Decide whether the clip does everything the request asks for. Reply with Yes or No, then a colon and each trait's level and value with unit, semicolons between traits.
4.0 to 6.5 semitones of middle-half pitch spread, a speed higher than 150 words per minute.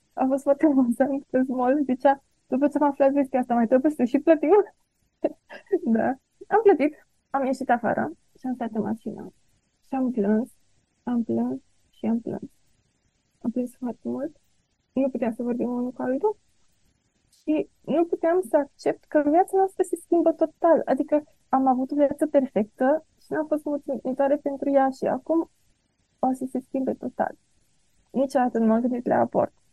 No: average, 3.6 semitones; fast, 170 wpm